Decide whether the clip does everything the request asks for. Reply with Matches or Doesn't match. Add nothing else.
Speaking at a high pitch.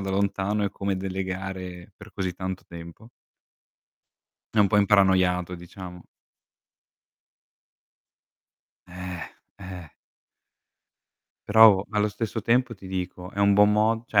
Doesn't match